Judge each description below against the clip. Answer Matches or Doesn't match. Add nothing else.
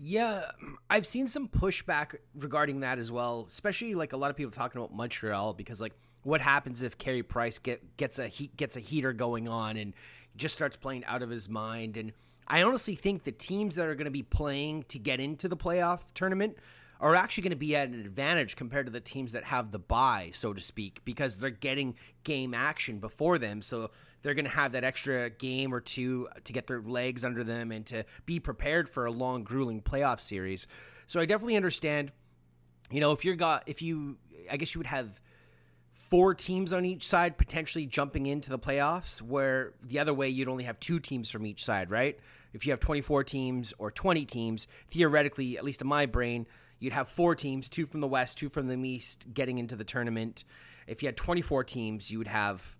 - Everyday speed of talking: Doesn't match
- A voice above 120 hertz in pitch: Matches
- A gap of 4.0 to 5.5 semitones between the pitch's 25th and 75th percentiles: Matches